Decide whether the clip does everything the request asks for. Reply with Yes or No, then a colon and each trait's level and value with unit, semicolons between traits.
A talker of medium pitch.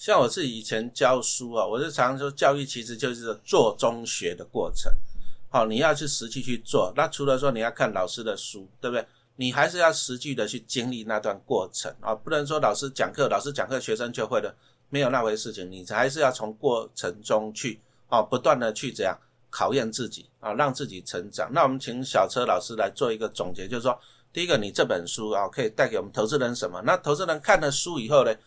No: low, 125 Hz